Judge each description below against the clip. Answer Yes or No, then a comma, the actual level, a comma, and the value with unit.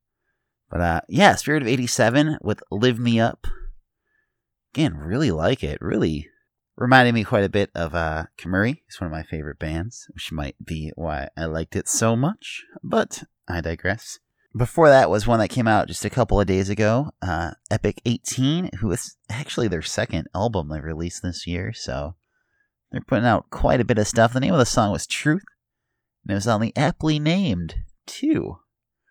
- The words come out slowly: No, average, 185 wpm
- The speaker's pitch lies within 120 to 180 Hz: No, low, 105 Hz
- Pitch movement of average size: No, wide, 6.8 semitones